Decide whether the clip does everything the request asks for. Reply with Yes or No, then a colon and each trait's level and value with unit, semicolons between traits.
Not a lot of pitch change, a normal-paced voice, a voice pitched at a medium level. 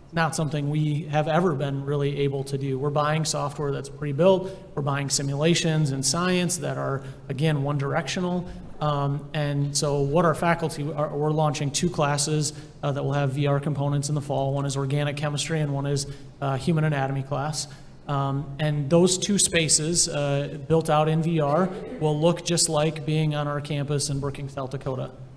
Yes: narrow, 1.9 semitones; average, 185 wpm; medium, 150 Hz